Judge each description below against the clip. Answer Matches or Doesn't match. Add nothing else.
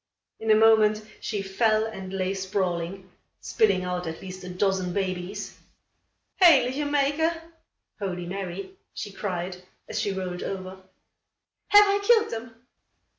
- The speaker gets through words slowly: Matches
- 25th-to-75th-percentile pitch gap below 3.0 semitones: Doesn't match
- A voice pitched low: Doesn't match